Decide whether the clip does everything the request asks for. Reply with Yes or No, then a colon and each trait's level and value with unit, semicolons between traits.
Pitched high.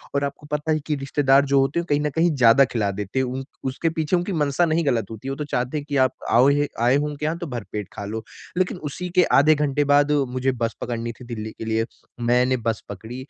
No: low, 135 Hz